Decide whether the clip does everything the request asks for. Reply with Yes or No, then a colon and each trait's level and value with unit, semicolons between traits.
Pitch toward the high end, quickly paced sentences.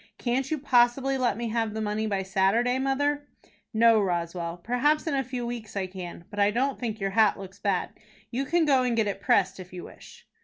Yes: high, 225 Hz; fast, 220 wpm